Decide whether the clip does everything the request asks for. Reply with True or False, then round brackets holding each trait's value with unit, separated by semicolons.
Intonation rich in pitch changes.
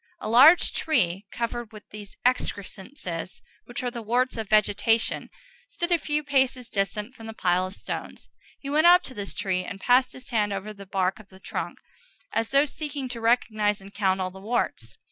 False (4.5 semitones)